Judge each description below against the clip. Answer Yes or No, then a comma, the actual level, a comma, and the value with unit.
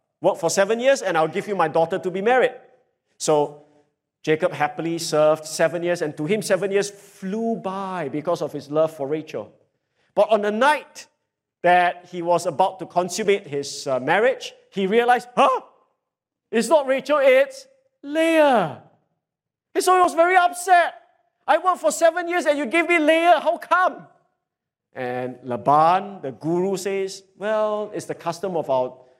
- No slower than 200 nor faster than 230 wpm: No, average, 165 wpm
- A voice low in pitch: No, high, 195 Hz